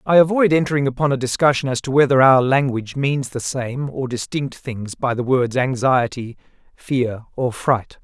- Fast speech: No, average, 180 wpm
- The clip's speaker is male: Yes, male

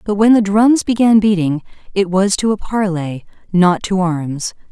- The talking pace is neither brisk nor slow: Yes, average, 180 wpm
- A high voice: Yes, high, 195 Hz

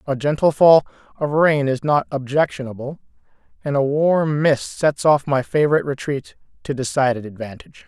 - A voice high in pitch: No, medium, 140 Hz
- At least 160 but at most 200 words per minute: No, average, 150 wpm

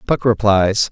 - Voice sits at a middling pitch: No, low, 105 Hz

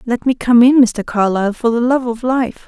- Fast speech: Yes, fast, 245 wpm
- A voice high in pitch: Yes, high, 240 Hz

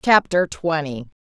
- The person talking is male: No, female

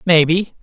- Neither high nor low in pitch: Yes, medium, 170 Hz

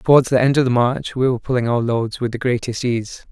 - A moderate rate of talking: No, fast, 270 wpm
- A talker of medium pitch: No, low, 125 Hz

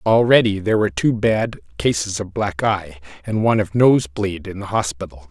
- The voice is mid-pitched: No, low, 110 Hz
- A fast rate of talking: No, average, 180 wpm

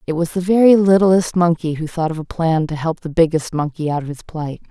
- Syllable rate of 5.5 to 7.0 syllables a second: Yes, 5.6 syllables/s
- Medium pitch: Yes, medium, 165 Hz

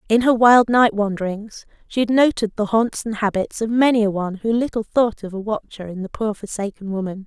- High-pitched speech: Yes, high, 215 Hz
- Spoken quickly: Yes, fast, 225 wpm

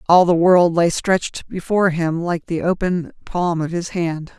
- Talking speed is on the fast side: No, average, 190 wpm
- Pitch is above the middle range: No, medium, 170 Hz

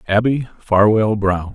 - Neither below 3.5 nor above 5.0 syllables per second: Yes, 3.9 syllables/s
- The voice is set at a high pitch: No, low, 105 Hz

